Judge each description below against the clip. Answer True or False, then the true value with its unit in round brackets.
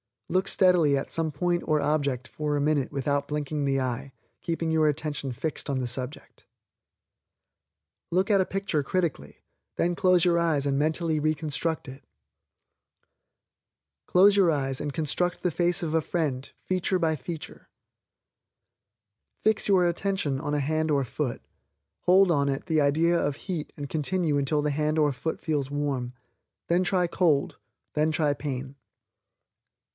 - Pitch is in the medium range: True (155 Hz)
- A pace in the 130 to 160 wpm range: True (155 wpm)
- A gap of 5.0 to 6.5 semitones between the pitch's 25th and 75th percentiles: False (3.4 semitones)